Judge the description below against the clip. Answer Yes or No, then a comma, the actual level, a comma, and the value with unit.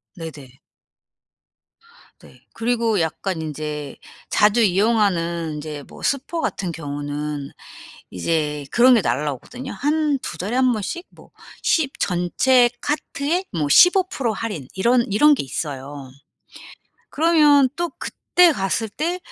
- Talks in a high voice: Yes, high, 200 Hz